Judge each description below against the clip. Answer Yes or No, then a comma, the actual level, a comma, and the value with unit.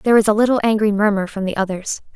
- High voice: Yes, high, 210 Hz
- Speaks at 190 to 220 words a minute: No, fast, 250 wpm